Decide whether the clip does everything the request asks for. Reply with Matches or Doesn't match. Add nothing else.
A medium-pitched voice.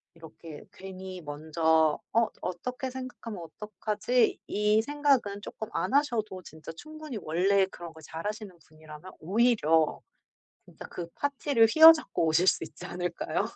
Doesn't match